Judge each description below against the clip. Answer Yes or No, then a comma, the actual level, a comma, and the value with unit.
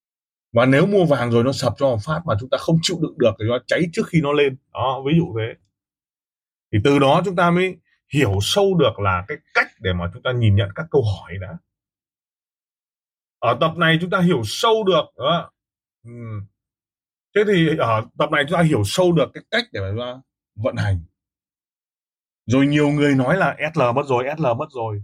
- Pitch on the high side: No, low, 135 Hz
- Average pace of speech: Yes, average, 210 wpm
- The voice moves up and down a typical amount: No, wide, 6.8 semitones